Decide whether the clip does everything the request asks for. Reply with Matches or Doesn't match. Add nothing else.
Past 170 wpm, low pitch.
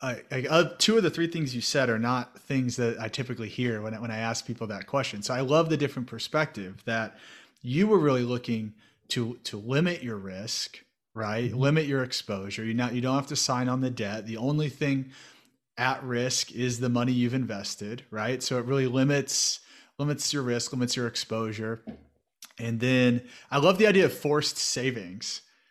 Matches